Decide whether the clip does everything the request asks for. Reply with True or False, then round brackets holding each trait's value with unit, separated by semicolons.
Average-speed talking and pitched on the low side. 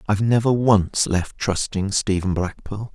True (165 wpm; 100 Hz)